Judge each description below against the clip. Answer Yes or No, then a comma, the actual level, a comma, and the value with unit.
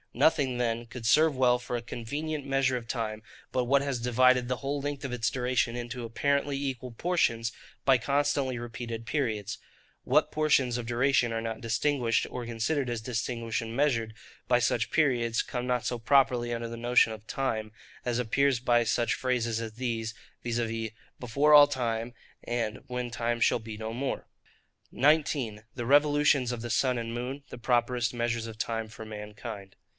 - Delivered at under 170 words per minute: No, average, 175 wpm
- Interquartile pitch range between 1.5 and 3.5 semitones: Yes, narrow, 2.5 semitones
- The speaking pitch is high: No, low, 120 Hz